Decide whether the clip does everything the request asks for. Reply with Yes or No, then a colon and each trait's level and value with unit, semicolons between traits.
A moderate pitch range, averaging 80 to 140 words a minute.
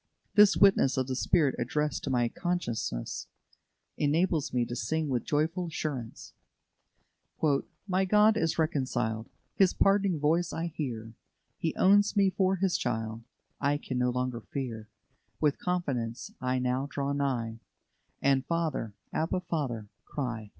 No: wide, 6.1 semitones; slow, 135 wpm